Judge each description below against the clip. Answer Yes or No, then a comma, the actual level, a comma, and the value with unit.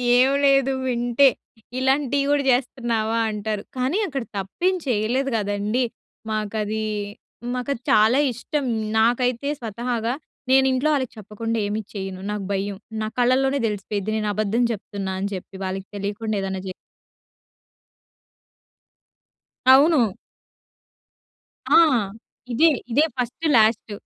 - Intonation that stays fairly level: No, average, 3.8 semitones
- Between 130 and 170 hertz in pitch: No, high, 230 Hz